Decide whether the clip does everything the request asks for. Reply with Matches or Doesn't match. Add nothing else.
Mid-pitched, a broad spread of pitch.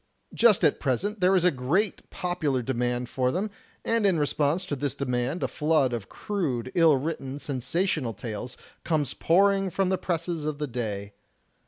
Matches